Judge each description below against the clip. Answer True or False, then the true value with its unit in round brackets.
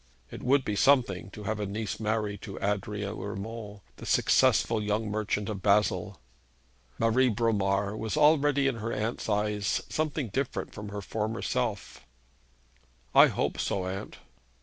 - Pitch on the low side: True (105 Hz)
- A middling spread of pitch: False (2.1 semitones)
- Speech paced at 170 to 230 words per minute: False (150 wpm)